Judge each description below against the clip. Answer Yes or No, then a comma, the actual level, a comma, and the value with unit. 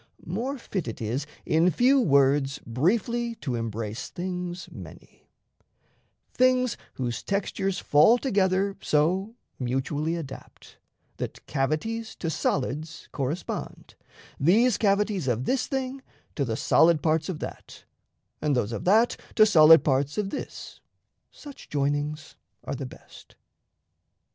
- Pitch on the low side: No, medium, 165 Hz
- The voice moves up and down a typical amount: No, wide, 6.9 semitones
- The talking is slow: Yes, slow, 125 wpm